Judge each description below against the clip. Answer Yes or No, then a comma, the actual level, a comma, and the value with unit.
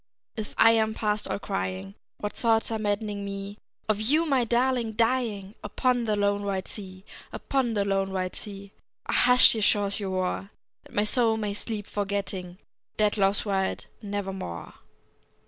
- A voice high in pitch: Yes, high, 205 Hz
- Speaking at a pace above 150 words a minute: Yes, average, 165 wpm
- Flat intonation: Yes, narrow, 2.2 semitones